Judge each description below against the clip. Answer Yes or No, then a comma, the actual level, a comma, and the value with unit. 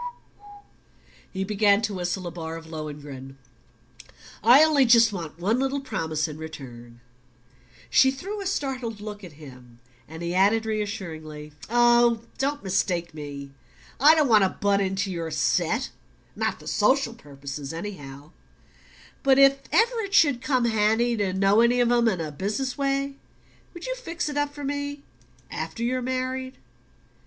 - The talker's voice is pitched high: Yes, high, 210 Hz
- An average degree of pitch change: No, wide, 8.4 semitones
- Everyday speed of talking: Yes, average, 155 wpm